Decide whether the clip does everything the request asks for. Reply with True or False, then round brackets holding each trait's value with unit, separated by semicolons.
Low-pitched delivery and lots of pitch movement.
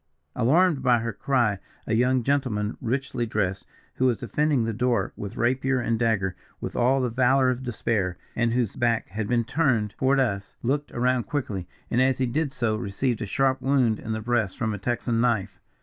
False (120 Hz; 3.0 semitones)